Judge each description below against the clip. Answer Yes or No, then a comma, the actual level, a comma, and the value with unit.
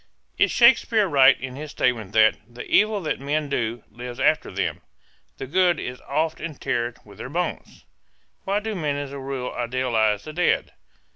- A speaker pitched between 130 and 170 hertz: Yes, medium, 140 Hz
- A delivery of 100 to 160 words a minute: No, average, 170 wpm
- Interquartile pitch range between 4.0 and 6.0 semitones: Yes, average, 5.2 semitones